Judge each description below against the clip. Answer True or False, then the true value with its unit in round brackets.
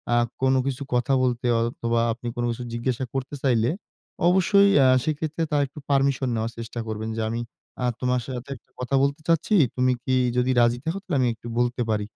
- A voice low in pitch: True (125 Hz)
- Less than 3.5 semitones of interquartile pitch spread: True (2.9 semitones)